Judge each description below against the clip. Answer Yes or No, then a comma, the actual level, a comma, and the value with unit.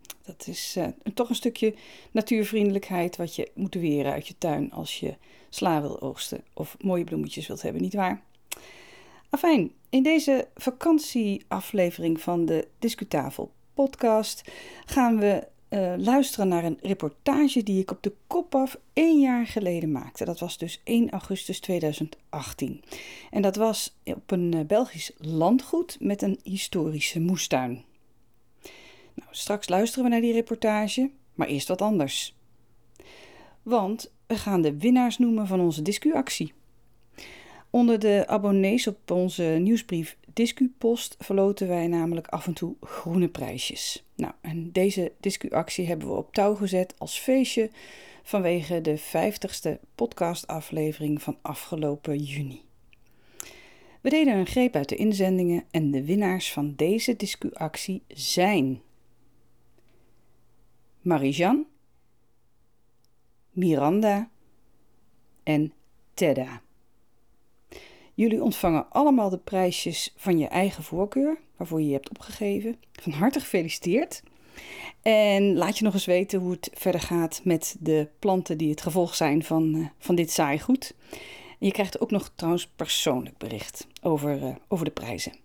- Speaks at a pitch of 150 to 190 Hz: Yes, medium, 185 Hz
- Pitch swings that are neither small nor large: No, wide, 6.4 semitones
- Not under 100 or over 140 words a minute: Yes, slow, 135 wpm